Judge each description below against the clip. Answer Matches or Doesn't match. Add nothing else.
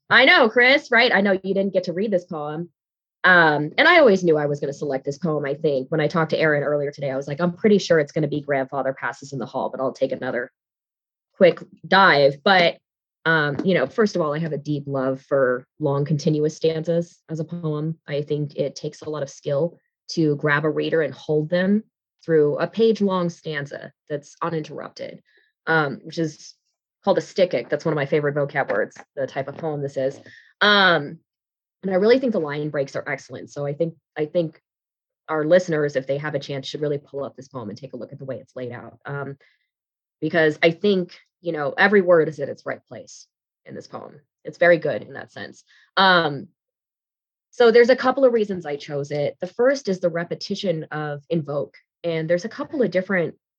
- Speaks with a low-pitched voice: Doesn't match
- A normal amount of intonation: Matches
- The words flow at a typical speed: Doesn't match